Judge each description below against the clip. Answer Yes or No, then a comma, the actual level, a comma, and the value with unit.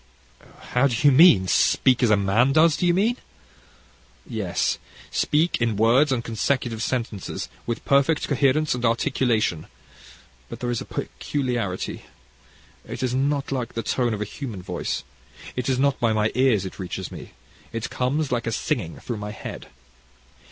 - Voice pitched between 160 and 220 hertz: No, low, 125 Hz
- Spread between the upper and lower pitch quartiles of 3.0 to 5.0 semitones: Yes, average, 3.9 semitones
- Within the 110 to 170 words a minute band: Yes, average, 165 wpm